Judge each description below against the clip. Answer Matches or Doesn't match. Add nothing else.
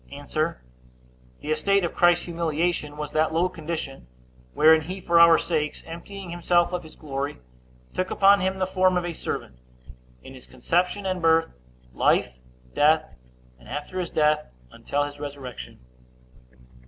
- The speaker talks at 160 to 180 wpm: Doesn't match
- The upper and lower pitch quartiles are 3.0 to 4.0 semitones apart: Matches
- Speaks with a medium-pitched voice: Matches